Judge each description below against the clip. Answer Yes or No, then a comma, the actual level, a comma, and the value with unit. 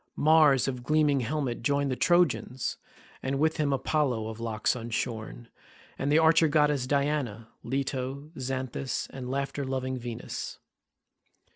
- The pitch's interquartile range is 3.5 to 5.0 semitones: No, average, 3.0 semitones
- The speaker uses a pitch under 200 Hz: Yes, low, 135 Hz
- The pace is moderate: No, slow, 130 wpm